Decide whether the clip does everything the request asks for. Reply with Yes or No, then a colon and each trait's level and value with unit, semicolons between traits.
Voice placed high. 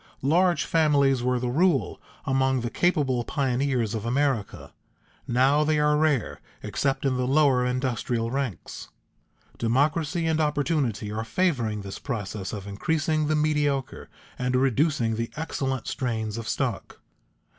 No: low, 135 Hz